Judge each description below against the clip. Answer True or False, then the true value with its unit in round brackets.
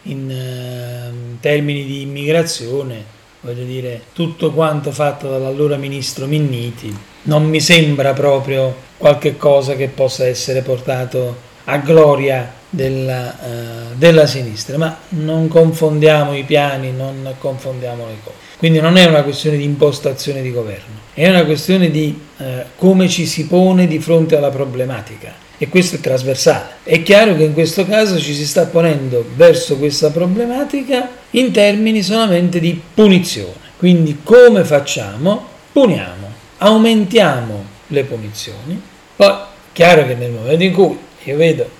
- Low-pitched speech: False (145 Hz)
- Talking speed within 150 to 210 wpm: False (140 wpm)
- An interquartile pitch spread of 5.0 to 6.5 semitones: False (4.5 semitones)